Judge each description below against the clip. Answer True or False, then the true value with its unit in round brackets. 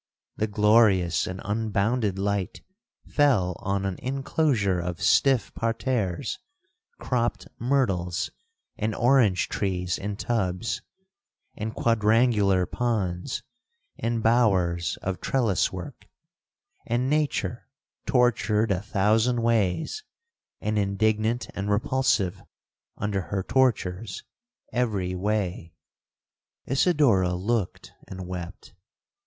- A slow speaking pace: True (95 wpm)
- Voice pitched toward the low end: True (105 Hz)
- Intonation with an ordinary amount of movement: True (4.1 semitones)